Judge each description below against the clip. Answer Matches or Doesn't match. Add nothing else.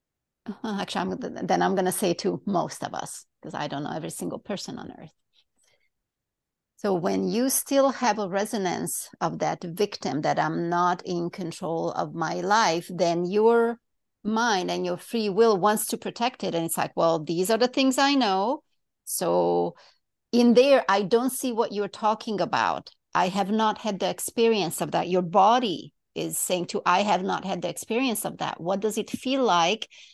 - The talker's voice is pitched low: Doesn't match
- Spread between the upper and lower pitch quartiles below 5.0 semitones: Matches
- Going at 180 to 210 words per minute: Matches